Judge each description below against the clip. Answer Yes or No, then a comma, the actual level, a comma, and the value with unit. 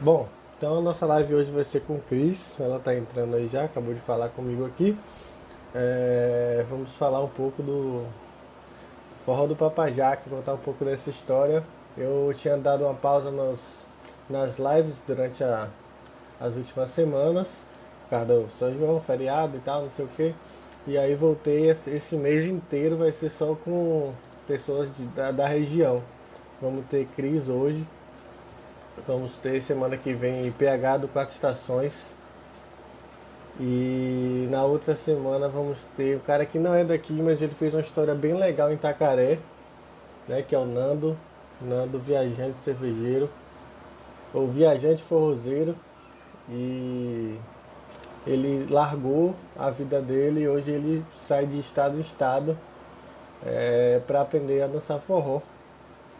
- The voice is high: No, medium, 140 Hz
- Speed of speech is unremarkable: Yes, average, 150 wpm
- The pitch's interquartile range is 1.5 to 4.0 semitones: Yes, average, 3.1 semitones